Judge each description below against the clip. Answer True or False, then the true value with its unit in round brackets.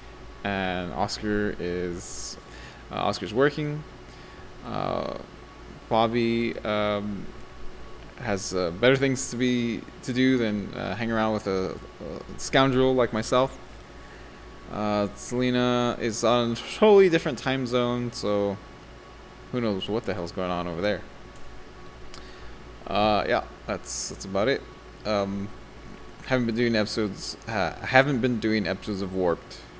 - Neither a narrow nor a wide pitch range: True (3.9 semitones)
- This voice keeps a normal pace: False (130 wpm)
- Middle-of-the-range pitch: False (110 Hz)